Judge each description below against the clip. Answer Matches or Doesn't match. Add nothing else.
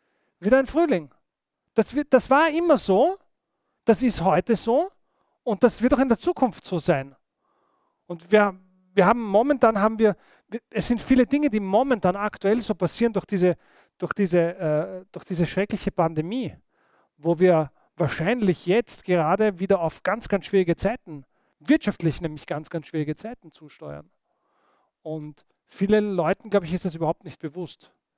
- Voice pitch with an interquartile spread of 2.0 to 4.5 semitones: Doesn't match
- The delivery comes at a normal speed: Matches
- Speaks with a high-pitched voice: Matches